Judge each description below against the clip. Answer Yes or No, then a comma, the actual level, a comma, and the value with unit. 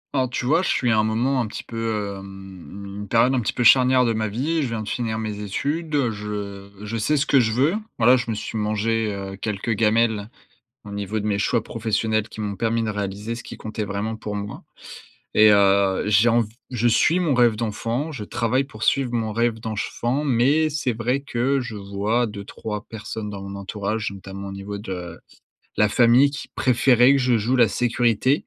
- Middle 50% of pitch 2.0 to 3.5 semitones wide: Yes, average, 3.0 semitones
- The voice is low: Yes, low, 110 Hz